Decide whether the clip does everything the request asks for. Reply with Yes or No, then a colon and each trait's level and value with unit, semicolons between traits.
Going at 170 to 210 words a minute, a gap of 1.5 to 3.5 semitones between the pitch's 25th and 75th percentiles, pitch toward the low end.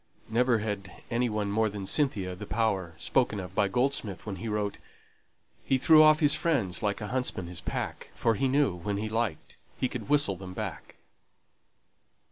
No: average, 180 wpm; average, 4.5 semitones; low, 110 Hz